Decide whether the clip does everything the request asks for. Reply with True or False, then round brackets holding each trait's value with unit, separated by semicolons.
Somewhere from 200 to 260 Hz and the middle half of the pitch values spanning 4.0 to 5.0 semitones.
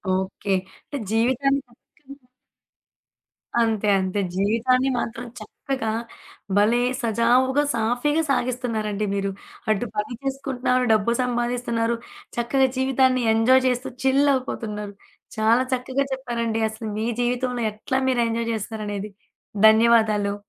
False (235 Hz; 2.9 semitones)